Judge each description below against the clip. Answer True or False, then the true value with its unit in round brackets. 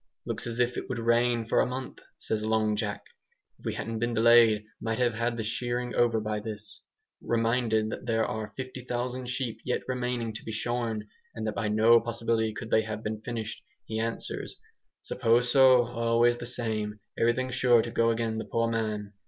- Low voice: True (115 Hz)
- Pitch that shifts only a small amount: True (1.6 semitones)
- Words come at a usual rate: True (190 wpm)